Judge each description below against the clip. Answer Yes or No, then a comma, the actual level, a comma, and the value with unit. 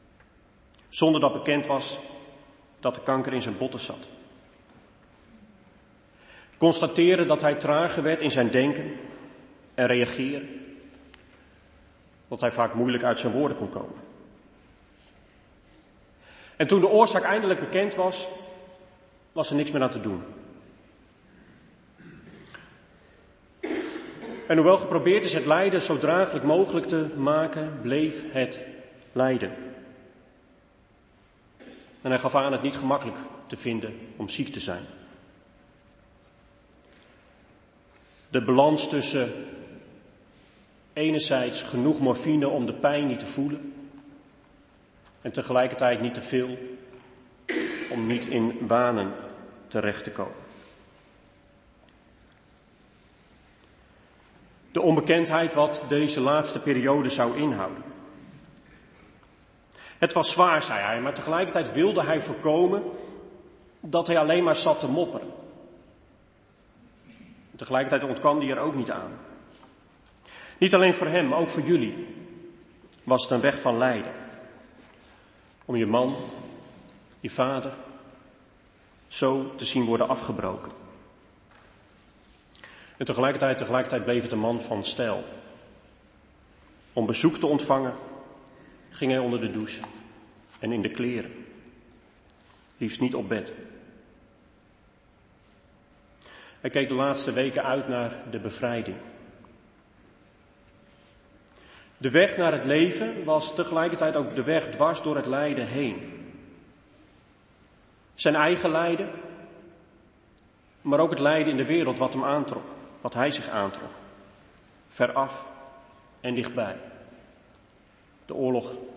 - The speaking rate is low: Yes, slow, 115 wpm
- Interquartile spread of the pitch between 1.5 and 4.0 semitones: No, average, 4.6 semitones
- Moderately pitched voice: No, low, 130 Hz